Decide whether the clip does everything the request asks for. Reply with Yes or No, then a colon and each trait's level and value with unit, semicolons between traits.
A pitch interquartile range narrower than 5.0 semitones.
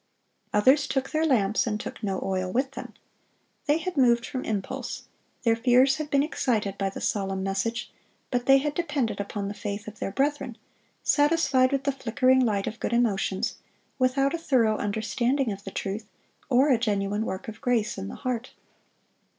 Yes: average, 4.6 semitones